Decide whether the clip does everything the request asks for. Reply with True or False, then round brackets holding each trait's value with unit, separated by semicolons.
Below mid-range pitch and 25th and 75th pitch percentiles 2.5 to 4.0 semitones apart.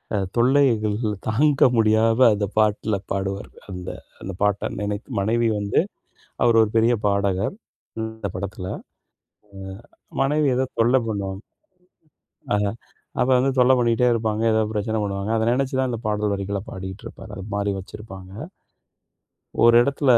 True (110 Hz; 2.8 semitones)